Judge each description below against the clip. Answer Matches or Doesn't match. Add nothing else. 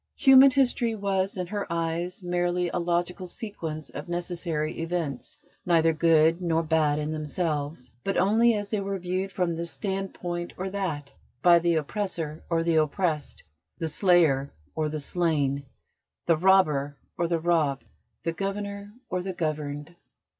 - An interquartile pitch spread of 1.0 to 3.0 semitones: Doesn't match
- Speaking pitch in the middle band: Matches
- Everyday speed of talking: Matches